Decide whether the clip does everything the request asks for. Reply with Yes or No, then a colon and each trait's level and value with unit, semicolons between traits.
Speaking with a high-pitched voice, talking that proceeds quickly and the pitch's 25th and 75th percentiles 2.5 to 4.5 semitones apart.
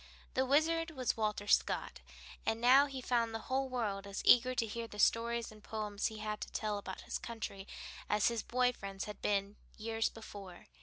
No: high, 225 Hz; average, 195 wpm; average, 3.0 semitones